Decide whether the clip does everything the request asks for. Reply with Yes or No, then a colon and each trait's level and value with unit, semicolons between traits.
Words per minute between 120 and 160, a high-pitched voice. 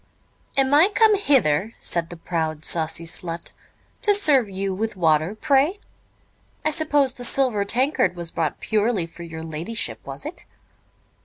Yes: average, 150 wpm; high, 210 Hz